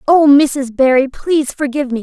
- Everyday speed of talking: Yes, average, 180 wpm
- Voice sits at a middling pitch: No, very high, 275 Hz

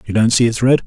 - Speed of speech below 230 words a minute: No, fast, 345 wpm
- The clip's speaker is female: No, male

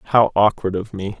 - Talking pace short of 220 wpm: Yes, average, 200 wpm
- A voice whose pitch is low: Yes, low, 100 Hz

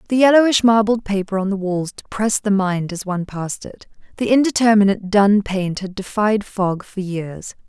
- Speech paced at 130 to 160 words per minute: No, average, 180 wpm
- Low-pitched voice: No, high, 205 Hz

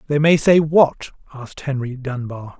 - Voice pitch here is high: No, medium, 140 Hz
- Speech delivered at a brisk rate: No, average, 160 wpm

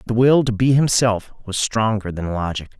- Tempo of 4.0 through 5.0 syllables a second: No, 5.2 syllables/s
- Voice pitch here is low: Yes, low, 110 Hz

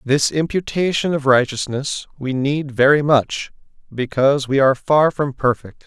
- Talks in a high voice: No, medium, 140 Hz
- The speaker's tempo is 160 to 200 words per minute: No, average, 145 wpm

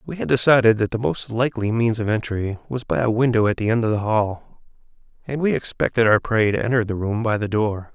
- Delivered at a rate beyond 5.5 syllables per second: Yes, 5.8 syllables/s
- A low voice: Yes, low, 115 Hz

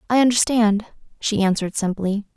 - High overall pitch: Yes, high, 215 Hz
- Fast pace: No, slow, 125 wpm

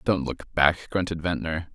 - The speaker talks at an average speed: Yes, average, 170 wpm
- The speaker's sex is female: No, male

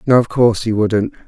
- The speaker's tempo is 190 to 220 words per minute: No, fast, 235 wpm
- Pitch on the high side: No, low, 110 Hz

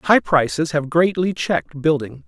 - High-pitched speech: No, medium, 155 Hz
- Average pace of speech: Yes, average, 160 wpm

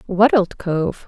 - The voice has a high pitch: Yes, high, 195 Hz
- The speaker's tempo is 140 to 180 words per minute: Yes, average, 170 wpm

